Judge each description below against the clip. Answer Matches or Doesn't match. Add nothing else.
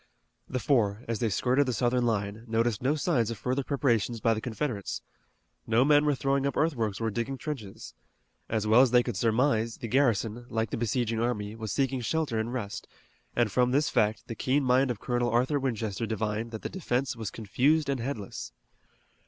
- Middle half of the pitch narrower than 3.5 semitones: Matches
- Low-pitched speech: Matches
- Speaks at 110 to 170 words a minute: Doesn't match